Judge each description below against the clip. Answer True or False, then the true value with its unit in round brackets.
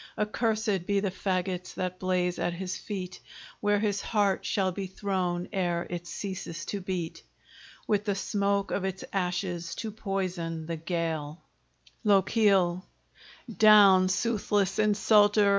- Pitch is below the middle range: False (190 Hz)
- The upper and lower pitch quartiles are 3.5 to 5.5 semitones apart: False (2.4 semitones)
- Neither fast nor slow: False (130 wpm)